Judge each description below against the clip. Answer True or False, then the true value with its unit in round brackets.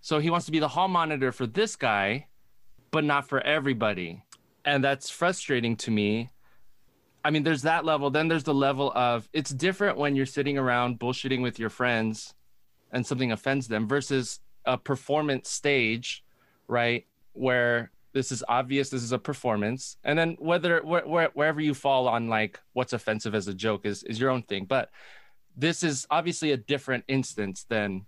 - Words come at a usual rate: True (180 wpm)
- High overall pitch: False (135 Hz)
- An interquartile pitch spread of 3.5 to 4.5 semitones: True (4.1 semitones)